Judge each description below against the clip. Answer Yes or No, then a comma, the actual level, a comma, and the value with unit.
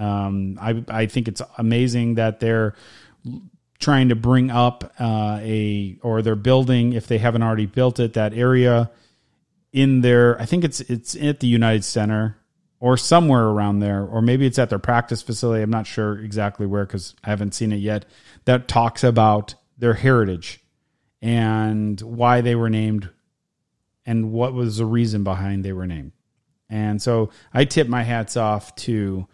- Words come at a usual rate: Yes, average, 170 wpm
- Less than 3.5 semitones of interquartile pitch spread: Yes, narrow, 2.6 semitones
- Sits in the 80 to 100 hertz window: No, low, 115 Hz